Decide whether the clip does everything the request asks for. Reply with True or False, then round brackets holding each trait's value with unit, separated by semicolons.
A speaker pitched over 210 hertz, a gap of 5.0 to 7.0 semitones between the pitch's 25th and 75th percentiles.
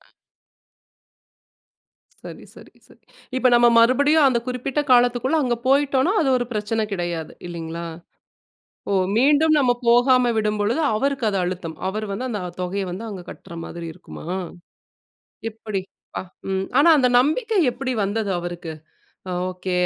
True (230 Hz; 5.4 semitones)